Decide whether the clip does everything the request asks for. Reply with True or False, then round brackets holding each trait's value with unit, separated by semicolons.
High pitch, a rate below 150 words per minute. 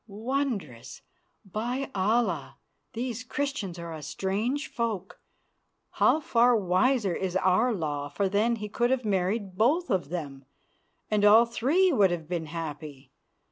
True (205 Hz; 140 wpm)